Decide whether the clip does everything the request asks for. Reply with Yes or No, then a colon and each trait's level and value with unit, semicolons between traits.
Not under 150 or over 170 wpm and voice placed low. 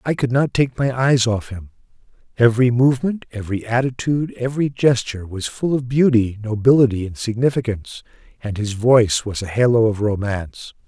Yes: average, 160 wpm; low, 120 Hz